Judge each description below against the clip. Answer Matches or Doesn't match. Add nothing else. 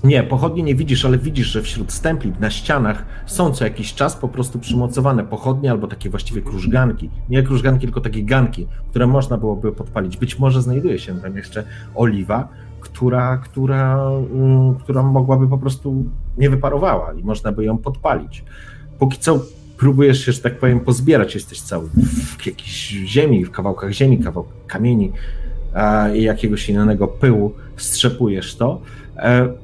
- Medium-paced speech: Matches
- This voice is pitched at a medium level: Doesn't match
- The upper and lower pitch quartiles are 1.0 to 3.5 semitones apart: Doesn't match